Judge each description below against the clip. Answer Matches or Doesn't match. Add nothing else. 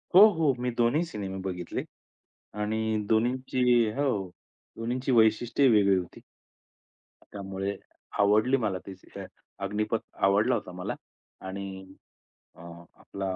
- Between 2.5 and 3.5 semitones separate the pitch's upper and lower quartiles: Doesn't match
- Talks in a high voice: Doesn't match